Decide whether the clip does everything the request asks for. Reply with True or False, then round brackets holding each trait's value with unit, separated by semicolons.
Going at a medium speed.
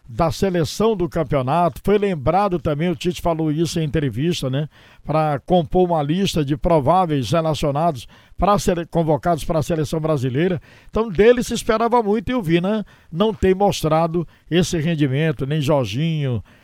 True (160 wpm)